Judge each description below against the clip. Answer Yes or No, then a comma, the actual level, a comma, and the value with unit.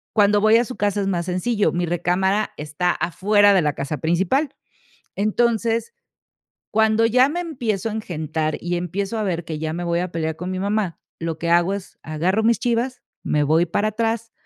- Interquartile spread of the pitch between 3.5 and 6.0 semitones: Yes, average, 4.4 semitones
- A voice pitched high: Yes, high, 195 Hz